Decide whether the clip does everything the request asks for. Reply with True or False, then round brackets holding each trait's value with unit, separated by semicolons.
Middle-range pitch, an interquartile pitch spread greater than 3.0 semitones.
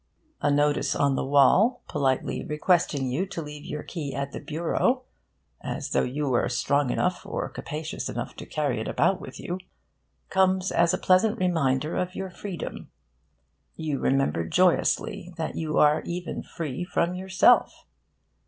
True (160 Hz; 4.4 semitones)